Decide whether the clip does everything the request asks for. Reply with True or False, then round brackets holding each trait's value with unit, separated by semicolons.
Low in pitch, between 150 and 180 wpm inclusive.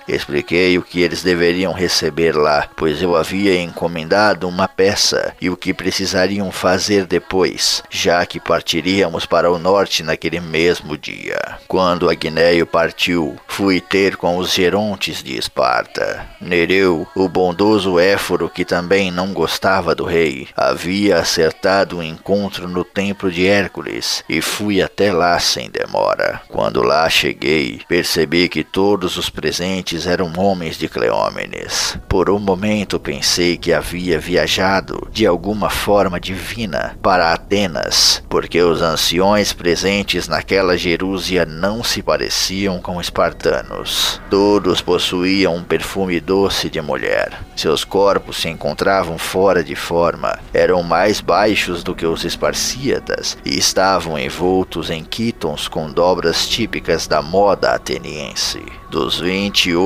False (90 Hz; 130 wpm)